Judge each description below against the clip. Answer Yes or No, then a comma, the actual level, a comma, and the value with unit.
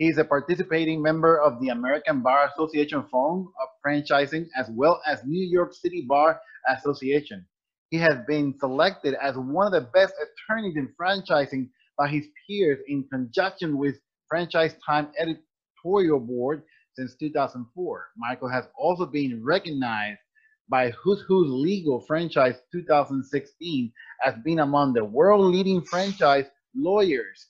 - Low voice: No, medium, 150 Hz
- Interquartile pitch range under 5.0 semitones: Yes, average, 4.4 semitones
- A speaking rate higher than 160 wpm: No, average, 140 wpm